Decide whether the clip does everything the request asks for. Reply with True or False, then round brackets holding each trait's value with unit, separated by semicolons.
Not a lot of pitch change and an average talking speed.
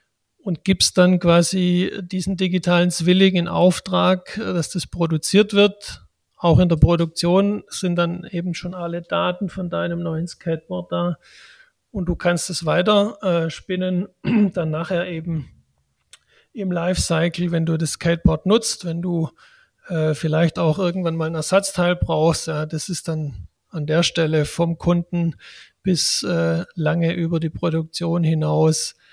True (2.1 semitones; 145 wpm)